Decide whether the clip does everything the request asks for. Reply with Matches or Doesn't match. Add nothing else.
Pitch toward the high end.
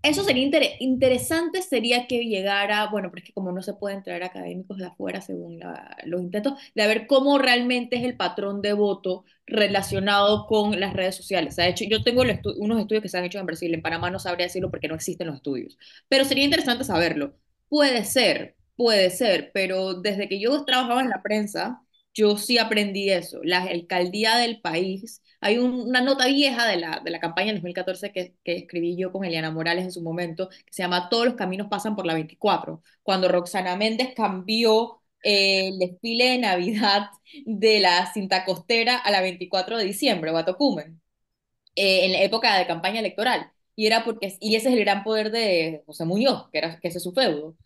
Matches